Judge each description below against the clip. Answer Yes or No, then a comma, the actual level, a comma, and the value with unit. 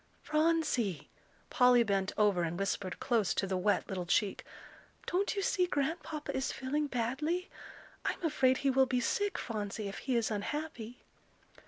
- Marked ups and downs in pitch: Yes, wide, 6.8 semitones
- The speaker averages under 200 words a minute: Yes, average, 155 wpm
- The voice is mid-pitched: No, very high, 250 Hz